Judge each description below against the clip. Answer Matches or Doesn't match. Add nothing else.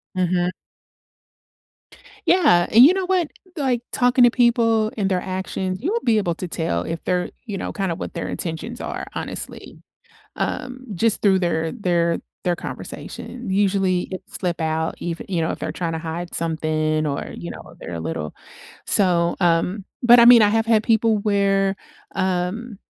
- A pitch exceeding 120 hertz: Matches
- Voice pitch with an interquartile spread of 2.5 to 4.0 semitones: Doesn't match